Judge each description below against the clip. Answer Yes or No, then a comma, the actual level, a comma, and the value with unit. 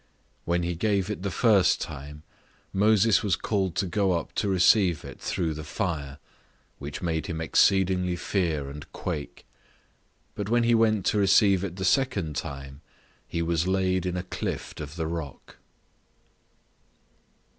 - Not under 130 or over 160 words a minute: Yes, average, 155 wpm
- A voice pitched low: Yes, very low, 90 Hz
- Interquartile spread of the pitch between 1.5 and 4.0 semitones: Yes, average, 3.7 semitones